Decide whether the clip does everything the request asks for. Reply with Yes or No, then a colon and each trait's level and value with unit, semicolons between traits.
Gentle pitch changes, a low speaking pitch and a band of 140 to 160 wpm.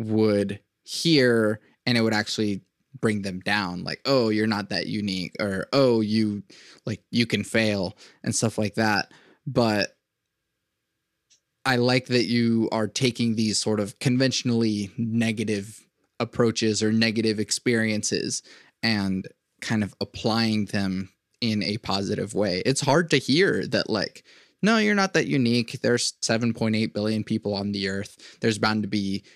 Yes: narrow, 2.3 semitones; low, 110 Hz; average, 150 wpm